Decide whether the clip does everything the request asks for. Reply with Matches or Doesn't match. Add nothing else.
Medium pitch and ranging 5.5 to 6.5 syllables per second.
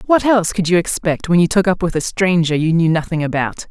Matches